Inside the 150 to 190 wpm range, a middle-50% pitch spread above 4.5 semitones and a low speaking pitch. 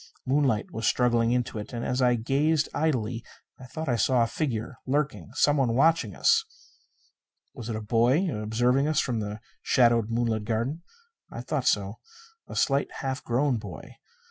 No: average, 165 wpm; average, 3.5 semitones; low, 125 Hz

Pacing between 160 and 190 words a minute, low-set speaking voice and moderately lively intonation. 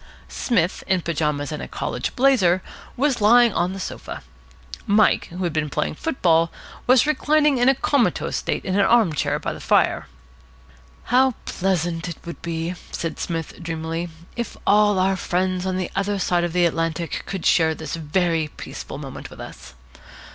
No: average, 170 wpm; medium, 180 Hz; average, 4.2 semitones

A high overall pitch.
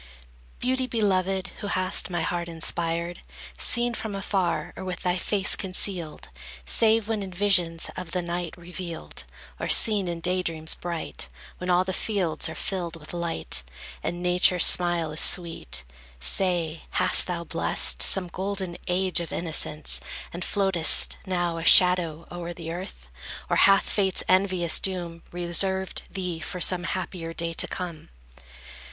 No: medium, 180 Hz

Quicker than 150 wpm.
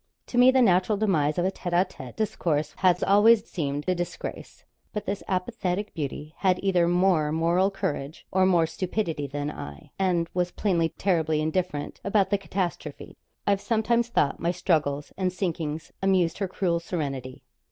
Yes: average, 165 wpm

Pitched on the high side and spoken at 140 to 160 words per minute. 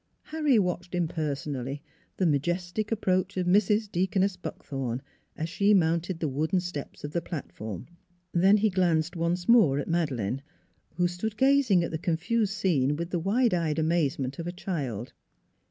No: medium, 175 Hz; average, 155 wpm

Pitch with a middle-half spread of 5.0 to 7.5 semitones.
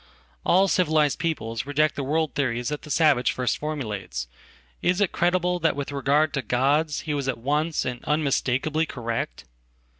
No: average, 3.6 semitones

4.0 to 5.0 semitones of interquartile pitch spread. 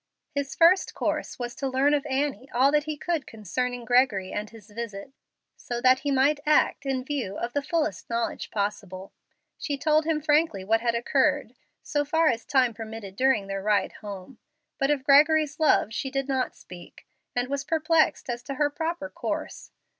Yes: average, 4.6 semitones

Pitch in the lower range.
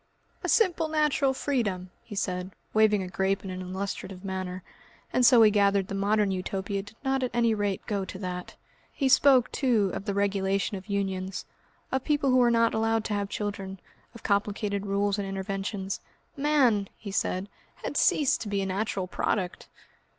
No: high, 200 Hz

